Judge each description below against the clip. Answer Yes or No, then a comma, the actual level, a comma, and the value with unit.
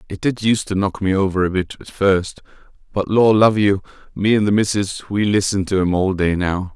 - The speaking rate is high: Yes, fast, 230 wpm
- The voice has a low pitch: Yes, low, 100 Hz